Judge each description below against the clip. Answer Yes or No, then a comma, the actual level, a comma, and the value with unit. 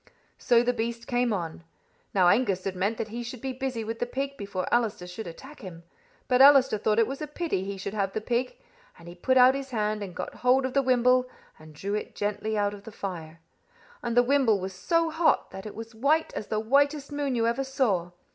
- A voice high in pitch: Yes, high, 230 Hz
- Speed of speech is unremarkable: No, fast, 235 wpm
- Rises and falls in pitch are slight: No, average, 4.7 semitones